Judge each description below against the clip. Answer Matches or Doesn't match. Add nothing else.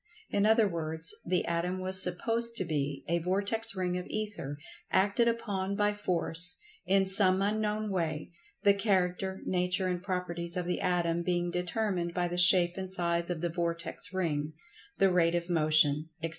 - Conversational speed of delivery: Matches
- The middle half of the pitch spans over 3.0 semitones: Doesn't match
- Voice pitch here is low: Doesn't match